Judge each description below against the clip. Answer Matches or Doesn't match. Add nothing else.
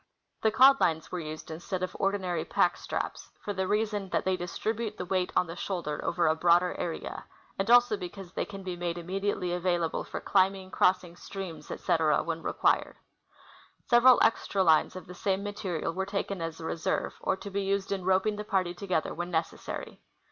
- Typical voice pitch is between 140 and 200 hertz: Matches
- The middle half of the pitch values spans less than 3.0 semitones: Matches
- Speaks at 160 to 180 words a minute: Doesn't match